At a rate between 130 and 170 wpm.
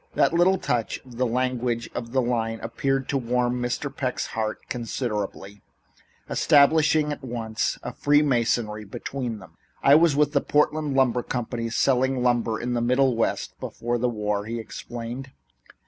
Yes: average, 160 wpm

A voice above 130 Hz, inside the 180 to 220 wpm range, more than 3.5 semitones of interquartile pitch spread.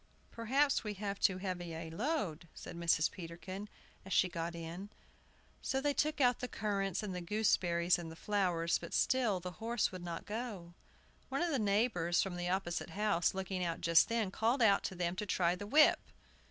Yes: high, 190 Hz; average, 195 wpm; average, 4.2 semitones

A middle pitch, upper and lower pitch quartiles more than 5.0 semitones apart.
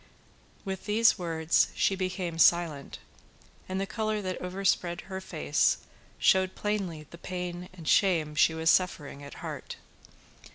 No: medium, 180 Hz; average, 2.8 semitones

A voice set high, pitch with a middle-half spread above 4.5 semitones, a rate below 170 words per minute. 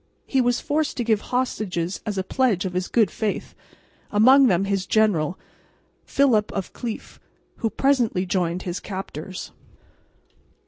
Yes: high, 210 Hz; average, 4.9 semitones; average, 140 wpm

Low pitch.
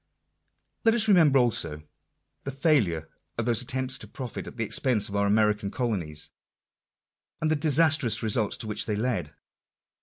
Yes: low, 115 Hz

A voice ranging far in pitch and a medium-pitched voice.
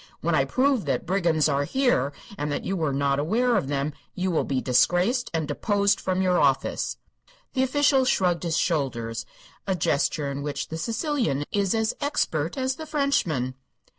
Yes: wide, 8.6 semitones; medium, 175 Hz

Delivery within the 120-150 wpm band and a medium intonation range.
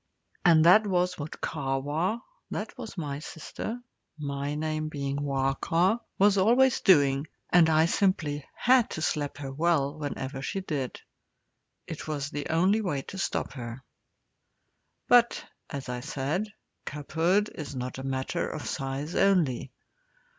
Yes: average, 140 wpm; average, 5.0 semitones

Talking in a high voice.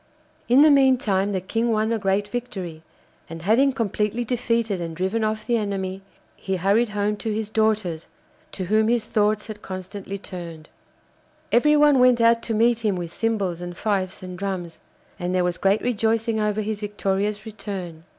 Yes: high, 210 Hz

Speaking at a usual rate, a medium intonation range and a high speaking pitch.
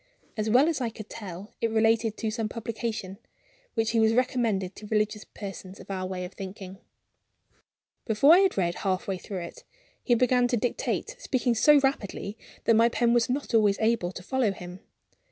Yes: average, 190 wpm; average, 3.6 semitones; high, 220 Hz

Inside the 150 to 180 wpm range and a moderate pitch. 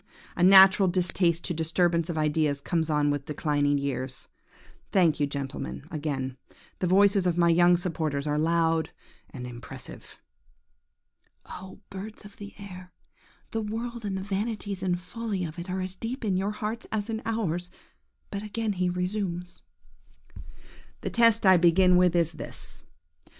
Yes: average, 155 wpm; medium, 180 Hz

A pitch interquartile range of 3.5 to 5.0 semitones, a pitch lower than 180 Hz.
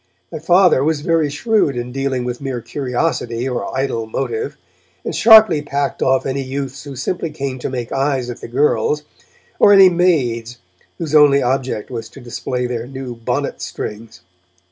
Yes: average, 3.9 semitones; low, 135 Hz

